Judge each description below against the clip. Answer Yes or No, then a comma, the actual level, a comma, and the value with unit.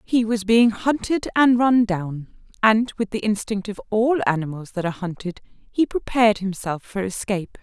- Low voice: No, high, 210 Hz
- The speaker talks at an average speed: Yes, average, 175 wpm